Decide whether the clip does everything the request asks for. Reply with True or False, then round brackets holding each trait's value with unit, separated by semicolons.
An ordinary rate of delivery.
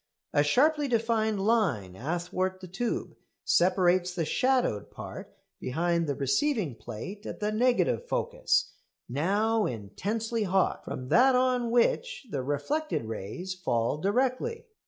False (125 wpm)